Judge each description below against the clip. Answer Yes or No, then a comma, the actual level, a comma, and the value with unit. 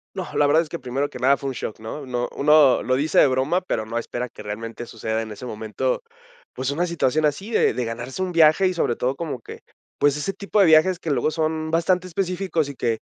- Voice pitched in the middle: Yes, medium, 145 Hz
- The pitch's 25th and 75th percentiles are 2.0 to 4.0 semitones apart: No, wide, 5.5 semitones